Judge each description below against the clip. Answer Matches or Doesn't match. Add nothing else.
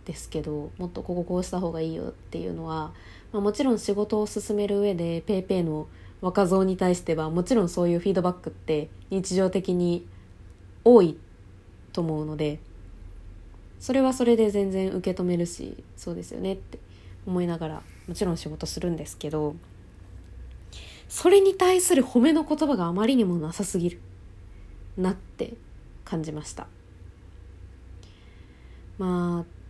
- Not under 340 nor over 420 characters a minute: Doesn't match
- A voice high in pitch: Doesn't match